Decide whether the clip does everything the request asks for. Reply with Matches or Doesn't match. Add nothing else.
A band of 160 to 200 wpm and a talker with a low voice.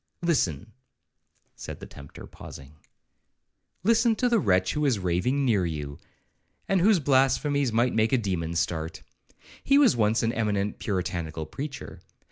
Doesn't match